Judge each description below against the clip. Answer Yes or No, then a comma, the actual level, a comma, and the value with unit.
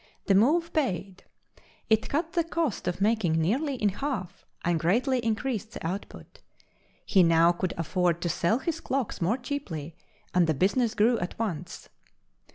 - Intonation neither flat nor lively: No, wide, 6.8 semitones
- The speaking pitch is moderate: No, high, 205 Hz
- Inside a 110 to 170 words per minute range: Yes, average, 160 wpm